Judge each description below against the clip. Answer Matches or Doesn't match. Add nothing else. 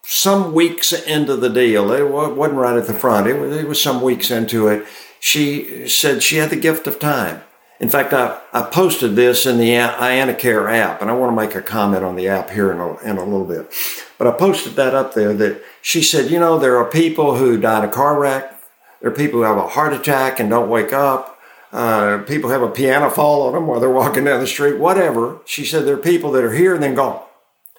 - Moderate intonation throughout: Matches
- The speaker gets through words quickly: Matches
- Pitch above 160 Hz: Doesn't match